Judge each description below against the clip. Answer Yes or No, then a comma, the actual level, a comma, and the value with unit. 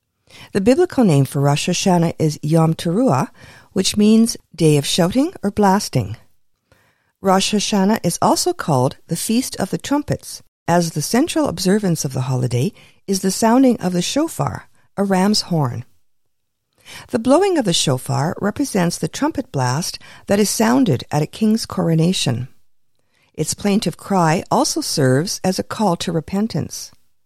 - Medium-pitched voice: Yes, medium, 175 Hz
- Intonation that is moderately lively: No, wide, 6.8 semitones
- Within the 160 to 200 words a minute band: No, average, 150 wpm